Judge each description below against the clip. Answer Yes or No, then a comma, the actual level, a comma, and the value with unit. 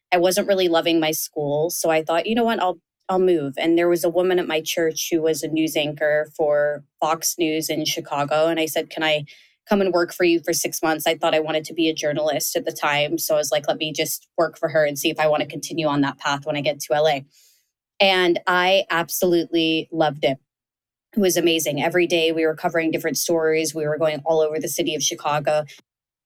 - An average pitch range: No, narrow, 2.0 semitones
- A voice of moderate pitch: Yes, medium, 160 Hz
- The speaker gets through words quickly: Yes, fast, 240 wpm